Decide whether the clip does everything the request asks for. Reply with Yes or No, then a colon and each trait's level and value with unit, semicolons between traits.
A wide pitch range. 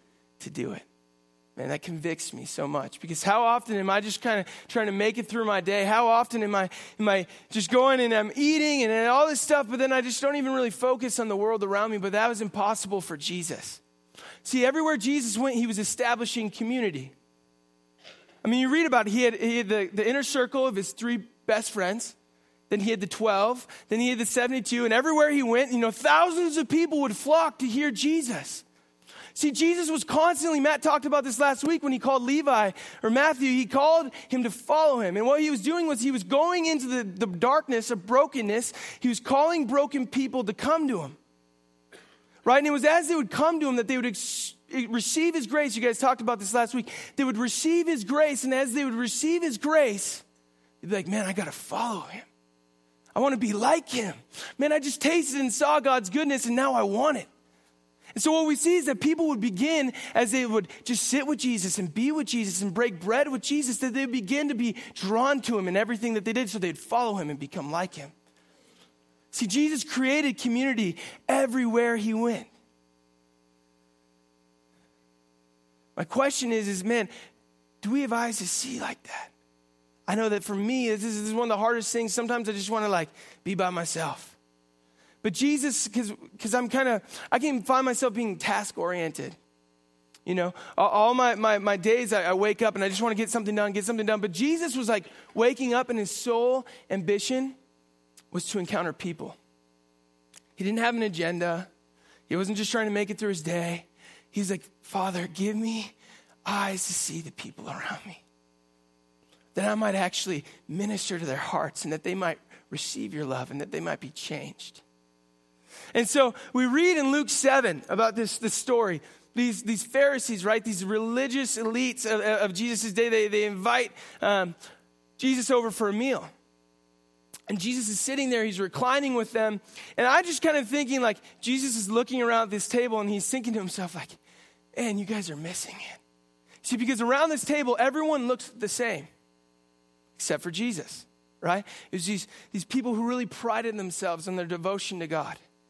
Yes: wide, 6.4 semitones